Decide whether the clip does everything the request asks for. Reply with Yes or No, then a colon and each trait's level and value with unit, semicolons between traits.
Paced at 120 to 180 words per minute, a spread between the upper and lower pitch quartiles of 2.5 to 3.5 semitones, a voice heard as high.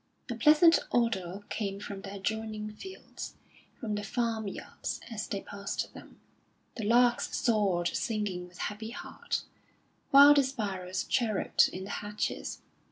Yes: average, 140 wpm; average, 3.0 semitones; high, 210 Hz